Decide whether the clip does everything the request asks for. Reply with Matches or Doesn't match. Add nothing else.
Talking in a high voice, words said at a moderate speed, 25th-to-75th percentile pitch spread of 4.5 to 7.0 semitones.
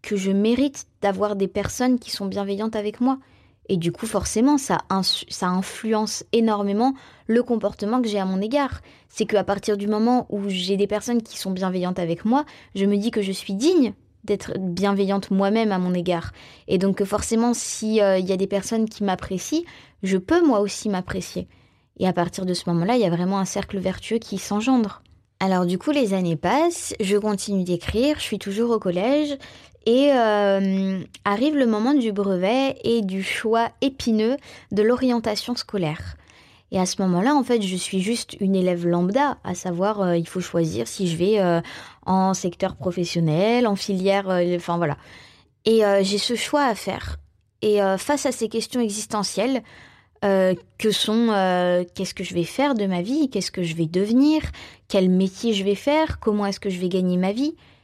Doesn't match